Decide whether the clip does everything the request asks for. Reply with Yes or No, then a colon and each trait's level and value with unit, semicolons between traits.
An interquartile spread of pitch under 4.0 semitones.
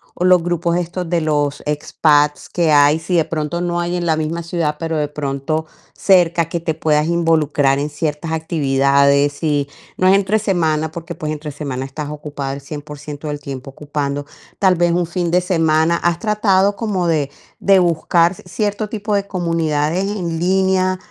Yes: average, 3.1 semitones